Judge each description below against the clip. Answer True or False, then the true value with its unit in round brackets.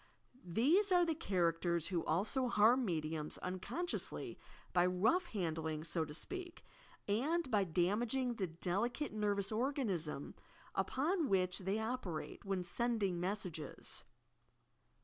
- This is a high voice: True (200 Hz)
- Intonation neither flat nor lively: False (6.5 semitones)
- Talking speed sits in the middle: False (130 wpm)